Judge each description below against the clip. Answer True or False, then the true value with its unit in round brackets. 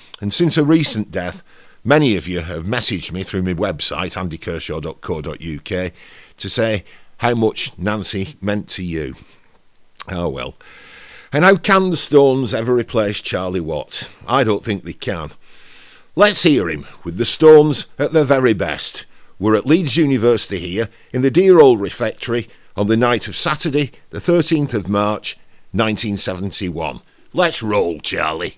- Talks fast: False (150 wpm)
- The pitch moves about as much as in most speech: False (7.0 semitones)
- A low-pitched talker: True (110 Hz)